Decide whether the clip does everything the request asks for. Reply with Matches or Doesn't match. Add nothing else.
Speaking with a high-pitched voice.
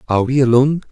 Doesn't match